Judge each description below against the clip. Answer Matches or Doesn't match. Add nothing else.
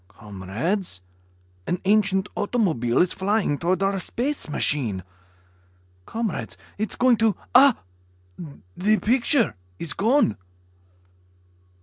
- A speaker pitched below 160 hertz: Doesn't match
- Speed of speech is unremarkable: Doesn't match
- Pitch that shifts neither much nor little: Doesn't match